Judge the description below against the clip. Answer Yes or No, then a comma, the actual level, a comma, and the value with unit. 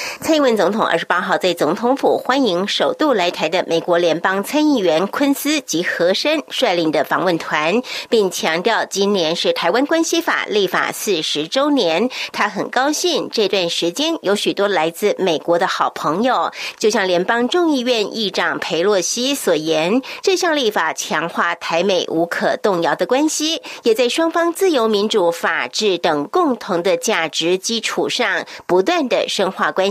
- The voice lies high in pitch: Yes, high, 225 Hz